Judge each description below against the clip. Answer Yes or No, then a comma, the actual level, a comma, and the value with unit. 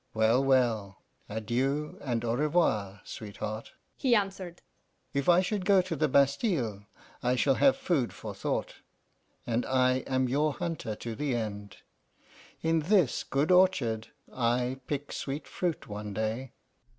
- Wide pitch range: Yes, wide, 6.3 semitones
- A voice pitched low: Yes, low, 130 Hz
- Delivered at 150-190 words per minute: No, average, 140 wpm